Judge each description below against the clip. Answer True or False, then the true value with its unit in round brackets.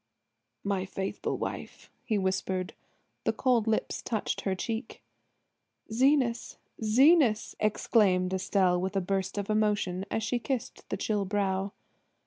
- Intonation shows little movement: False (3.1 semitones)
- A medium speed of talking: False (125 wpm)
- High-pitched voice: True (205 Hz)